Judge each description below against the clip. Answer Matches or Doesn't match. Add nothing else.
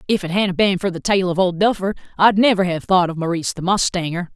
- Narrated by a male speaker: Doesn't match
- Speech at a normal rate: Doesn't match